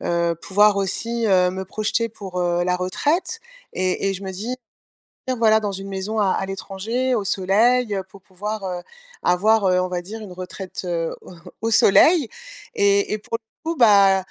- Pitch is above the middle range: Yes, high, 195 Hz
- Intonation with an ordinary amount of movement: Yes, average, 3.0 semitones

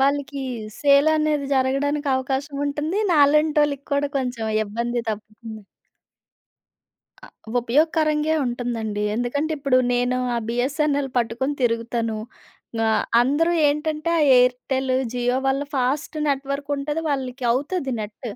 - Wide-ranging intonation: No, average, 3.1 semitones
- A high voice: Yes, very high, 270 Hz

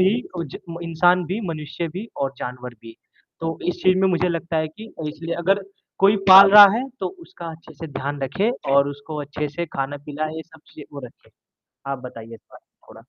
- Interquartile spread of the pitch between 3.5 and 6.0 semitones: Yes, average, 4.2 semitones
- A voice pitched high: No, medium, 160 Hz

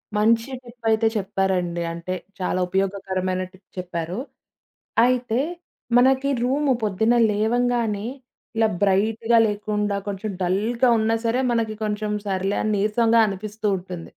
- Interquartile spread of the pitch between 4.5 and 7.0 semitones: No, average, 3.2 semitones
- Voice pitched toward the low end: No, high, 210 Hz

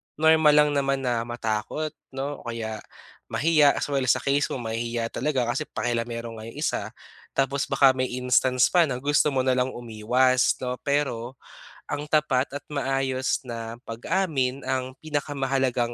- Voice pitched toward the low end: Yes, low, 130 Hz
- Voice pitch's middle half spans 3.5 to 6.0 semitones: No, average, 3.0 semitones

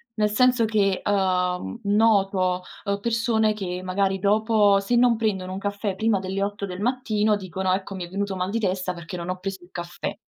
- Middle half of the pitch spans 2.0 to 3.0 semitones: Yes, narrow, 2.4 semitones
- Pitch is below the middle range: No, high, 200 Hz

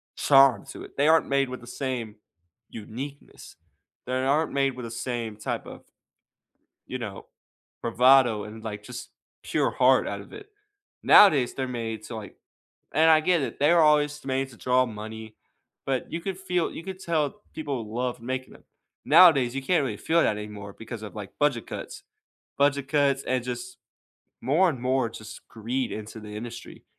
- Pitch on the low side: Yes, low, 130 Hz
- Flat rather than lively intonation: No, average, 4.3 semitones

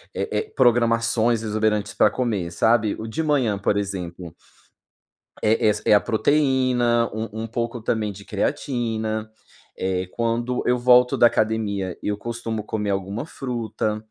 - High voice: No, low, 110 Hz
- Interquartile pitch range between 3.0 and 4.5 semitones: No, narrow, 2.4 semitones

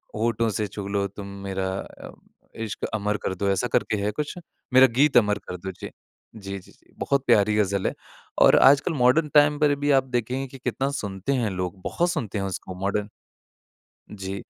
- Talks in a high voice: No, low, 105 Hz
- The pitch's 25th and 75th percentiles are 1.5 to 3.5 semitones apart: No, average, 5.2 semitones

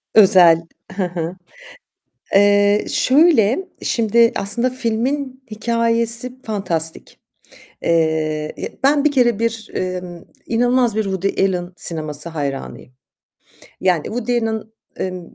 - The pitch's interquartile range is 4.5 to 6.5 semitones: Yes, average, 5.1 semitones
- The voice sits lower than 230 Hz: Yes, high, 210 Hz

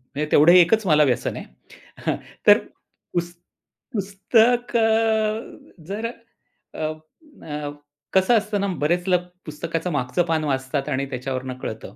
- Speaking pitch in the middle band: Yes, medium, 170 Hz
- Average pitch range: No, wide, 5.7 semitones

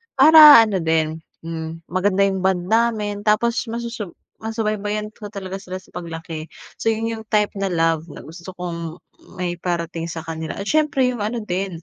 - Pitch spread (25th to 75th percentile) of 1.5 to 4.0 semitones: No, average, 4.6 semitones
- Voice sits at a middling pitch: No, high, 195 Hz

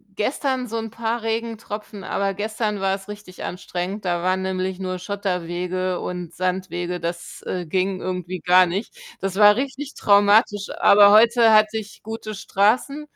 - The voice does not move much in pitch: No, average, 3.0 semitones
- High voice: Yes, high, 200 Hz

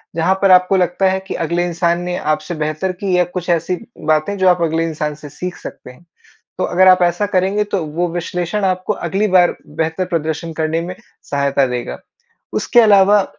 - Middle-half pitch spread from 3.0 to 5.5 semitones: No, narrow, 2.6 semitones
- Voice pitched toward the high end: No, medium, 175 Hz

